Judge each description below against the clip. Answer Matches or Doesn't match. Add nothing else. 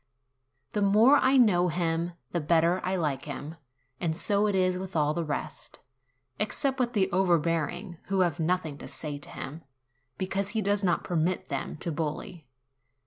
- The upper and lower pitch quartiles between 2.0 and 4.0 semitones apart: Matches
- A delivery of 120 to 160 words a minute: Doesn't match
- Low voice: Doesn't match